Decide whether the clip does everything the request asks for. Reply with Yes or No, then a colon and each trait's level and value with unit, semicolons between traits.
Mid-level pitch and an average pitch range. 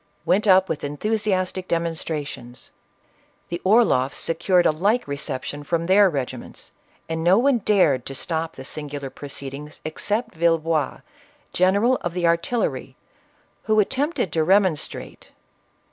Yes: medium, 170 Hz; average, 5.0 semitones